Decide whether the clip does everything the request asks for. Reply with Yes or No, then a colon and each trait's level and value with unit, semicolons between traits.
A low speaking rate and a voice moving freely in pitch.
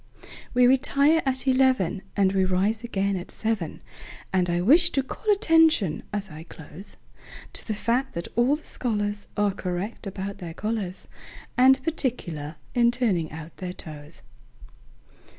Yes: slow, 130 wpm; wide, 6.1 semitones